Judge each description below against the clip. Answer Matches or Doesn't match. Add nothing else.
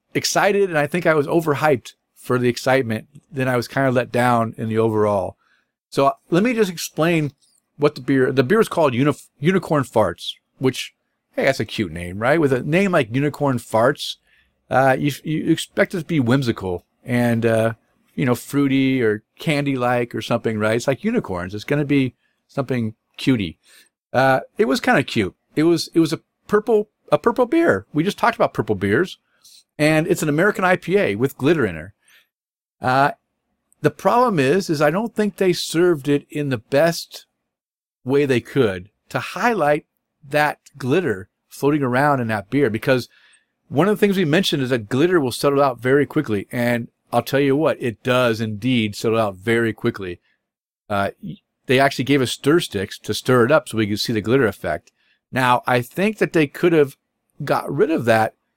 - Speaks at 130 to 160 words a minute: Doesn't match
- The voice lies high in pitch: Doesn't match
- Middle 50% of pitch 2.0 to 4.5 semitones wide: Doesn't match